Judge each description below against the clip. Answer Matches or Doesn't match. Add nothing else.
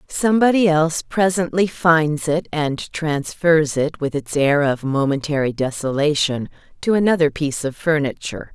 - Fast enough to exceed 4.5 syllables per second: Matches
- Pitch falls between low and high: Matches